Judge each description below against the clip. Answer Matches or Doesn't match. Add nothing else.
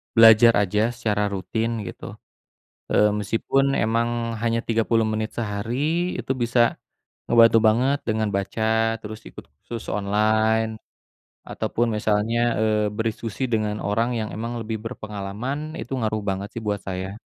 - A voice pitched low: Matches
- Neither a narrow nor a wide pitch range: Doesn't match